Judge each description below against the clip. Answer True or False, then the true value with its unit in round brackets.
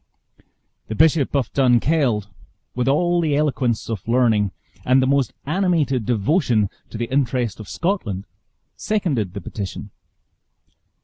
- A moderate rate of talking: False (125 wpm)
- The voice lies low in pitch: True (125 Hz)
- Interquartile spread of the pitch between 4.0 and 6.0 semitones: True (5.3 semitones)